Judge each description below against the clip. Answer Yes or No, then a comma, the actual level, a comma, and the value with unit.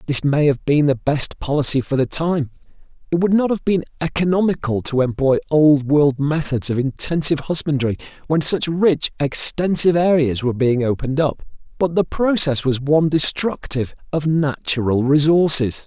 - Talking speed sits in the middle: Yes, average, 160 wpm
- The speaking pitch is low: No, medium, 150 Hz